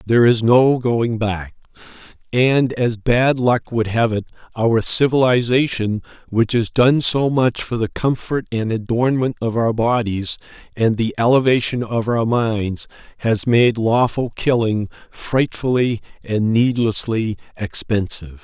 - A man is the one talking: Yes, male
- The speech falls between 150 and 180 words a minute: No, slow, 135 wpm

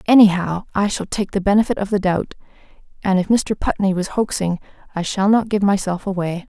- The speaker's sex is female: Yes, female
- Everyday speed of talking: Yes, average, 190 wpm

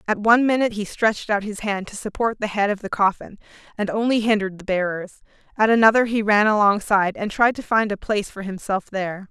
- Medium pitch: No, high, 210 Hz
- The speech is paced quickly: Yes, fast, 220 wpm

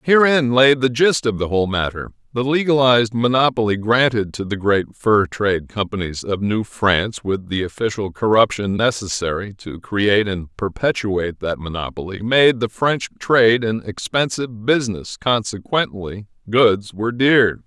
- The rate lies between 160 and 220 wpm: No, average, 145 wpm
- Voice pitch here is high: No, low, 110 Hz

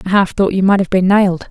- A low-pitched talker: No, high, 190 Hz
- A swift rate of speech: Yes, fast, 320 wpm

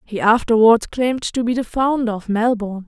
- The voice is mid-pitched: No, high, 230 Hz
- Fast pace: No, average, 190 wpm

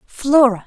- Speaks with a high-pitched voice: Yes, very high, 250 Hz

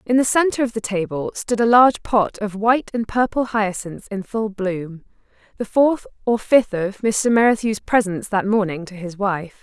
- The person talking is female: Yes, female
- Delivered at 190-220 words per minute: Yes, average, 195 wpm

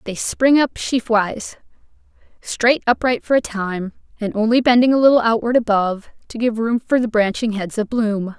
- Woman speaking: Yes, female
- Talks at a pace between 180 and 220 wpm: Yes, average, 185 wpm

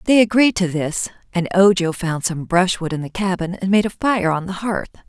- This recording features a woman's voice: Yes, female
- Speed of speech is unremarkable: No, fast, 225 wpm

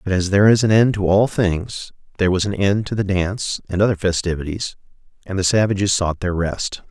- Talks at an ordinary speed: No, fast, 215 wpm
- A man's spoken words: Yes, male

